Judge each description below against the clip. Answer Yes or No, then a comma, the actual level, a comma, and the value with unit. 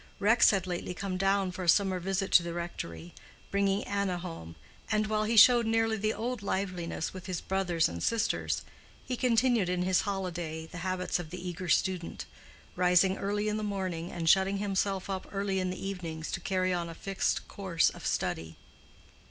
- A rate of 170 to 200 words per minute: Yes, average, 185 wpm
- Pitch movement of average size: No, narrow, 2.3 semitones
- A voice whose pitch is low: No, high, 190 Hz